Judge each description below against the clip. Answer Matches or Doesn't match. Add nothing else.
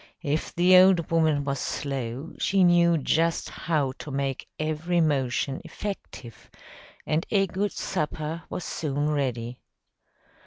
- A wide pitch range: Doesn't match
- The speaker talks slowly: Matches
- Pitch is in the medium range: Matches